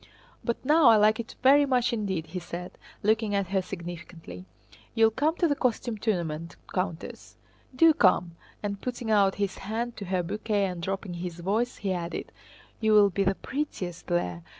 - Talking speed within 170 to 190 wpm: Yes, average, 175 wpm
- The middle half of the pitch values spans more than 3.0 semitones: Yes, average, 4.5 semitones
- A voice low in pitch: No, high, 200 Hz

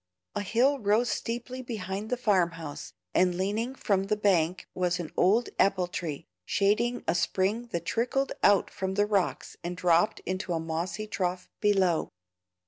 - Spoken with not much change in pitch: No, average, 3.5 semitones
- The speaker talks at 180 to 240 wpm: No, average, 160 wpm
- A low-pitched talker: No, high, 195 Hz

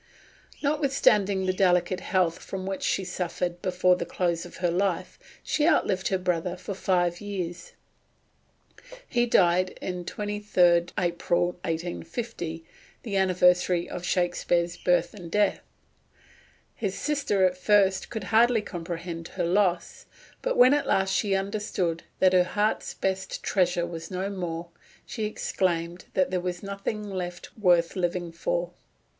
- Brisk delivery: No, average, 140 wpm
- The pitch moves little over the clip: Yes, narrow, 2.3 semitones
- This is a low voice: No, medium, 185 Hz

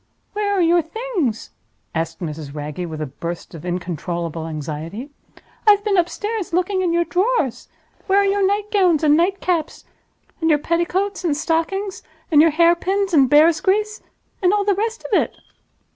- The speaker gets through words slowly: No, average, 175 wpm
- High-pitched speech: Yes, very high, 340 Hz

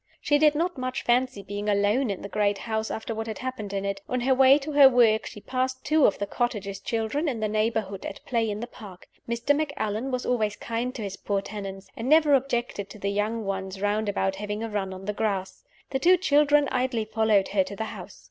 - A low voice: No, high, 220 Hz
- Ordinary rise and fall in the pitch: Yes, average, 4.1 semitones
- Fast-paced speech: Yes, fast, 235 wpm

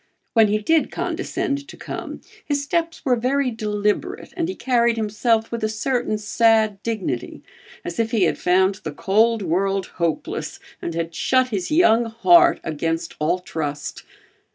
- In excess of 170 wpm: No, average, 155 wpm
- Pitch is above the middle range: Yes, high, 220 Hz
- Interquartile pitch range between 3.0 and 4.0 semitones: No, average, 5.1 semitones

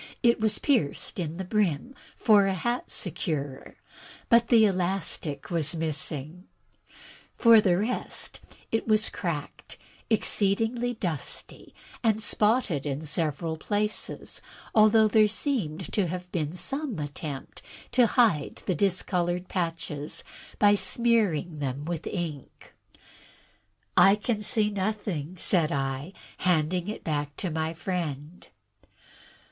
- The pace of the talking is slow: Yes, slow, 120 wpm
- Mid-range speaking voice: Yes, medium, 180 Hz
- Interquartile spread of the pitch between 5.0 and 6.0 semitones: Yes, wide, 5.5 semitones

